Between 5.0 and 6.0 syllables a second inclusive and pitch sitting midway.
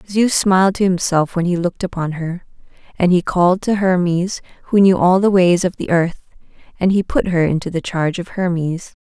Yes: 5.4 syllables/s; medium, 180 Hz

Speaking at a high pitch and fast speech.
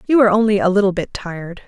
Yes: high, 200 Hz; fast, 250 wpm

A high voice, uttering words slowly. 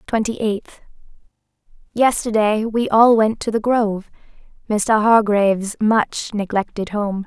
Yes: high, 215 Hz; slow, 105 wpm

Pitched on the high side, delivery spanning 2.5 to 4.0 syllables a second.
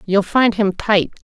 Yes: high, 200 Hz; 3.9 syllables/s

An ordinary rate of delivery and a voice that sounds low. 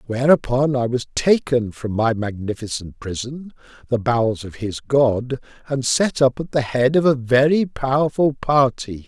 Yes: average, 160 wpm; low, 125 Hz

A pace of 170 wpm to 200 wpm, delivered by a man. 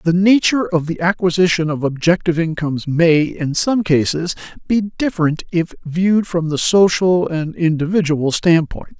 No: average, 145 wpm; male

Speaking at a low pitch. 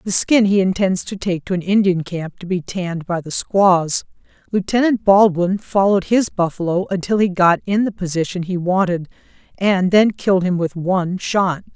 No: medium, 185 Hz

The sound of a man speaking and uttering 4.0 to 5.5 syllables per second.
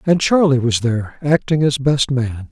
Yes: male; 4.8 syllables/s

